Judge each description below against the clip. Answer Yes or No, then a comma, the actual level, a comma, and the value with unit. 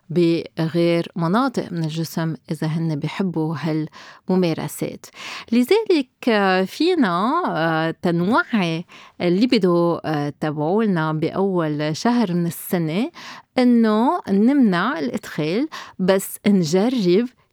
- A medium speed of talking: Yes, average, 80 wpm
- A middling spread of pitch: No, wide, 6.2 semitones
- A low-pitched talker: No, medium, 185 Hz